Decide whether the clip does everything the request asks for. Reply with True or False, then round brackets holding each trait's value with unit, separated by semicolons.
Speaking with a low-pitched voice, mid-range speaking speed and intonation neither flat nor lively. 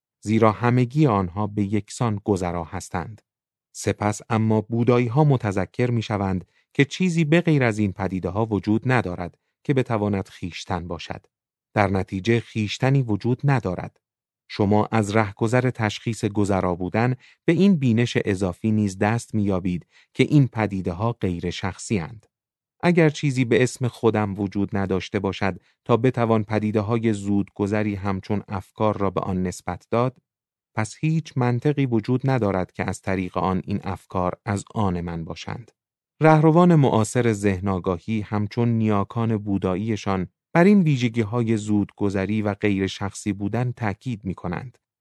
True (110 Hz; 145 wpm; 3.8 semitones)